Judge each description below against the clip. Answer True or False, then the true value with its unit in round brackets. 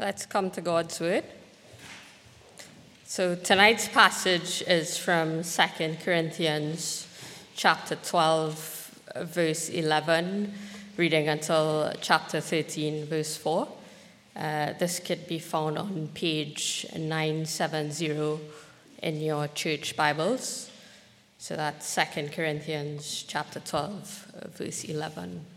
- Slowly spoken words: True (100 wpm)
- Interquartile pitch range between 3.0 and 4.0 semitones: False (2.5 semitones)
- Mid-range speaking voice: True (160 Hz)